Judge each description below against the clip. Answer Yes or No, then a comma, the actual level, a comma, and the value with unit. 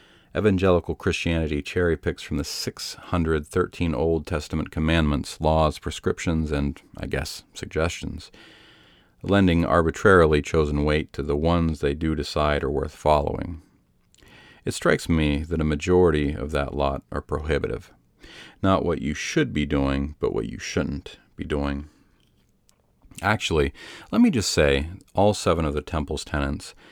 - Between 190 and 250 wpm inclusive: No, average, 140 wpm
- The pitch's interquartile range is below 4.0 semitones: Yes, average, 2.9 semitones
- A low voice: Yes, very low, 80 Hz